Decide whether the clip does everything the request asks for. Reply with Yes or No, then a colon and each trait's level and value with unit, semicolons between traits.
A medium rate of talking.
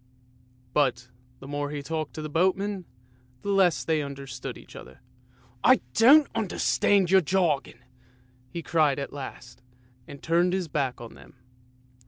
Yes: average, 155 wpm